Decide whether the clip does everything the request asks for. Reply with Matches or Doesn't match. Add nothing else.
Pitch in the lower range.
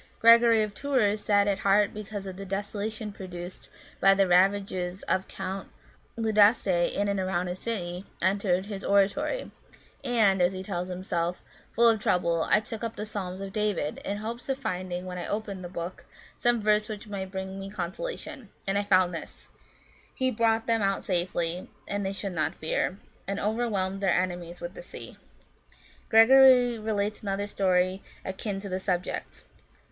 Doesn't match